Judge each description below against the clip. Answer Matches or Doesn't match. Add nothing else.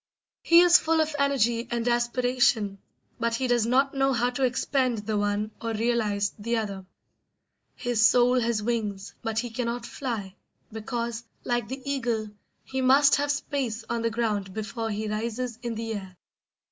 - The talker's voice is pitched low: Doesn't match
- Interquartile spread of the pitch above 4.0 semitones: Doesn't match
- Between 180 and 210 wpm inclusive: Doesn't match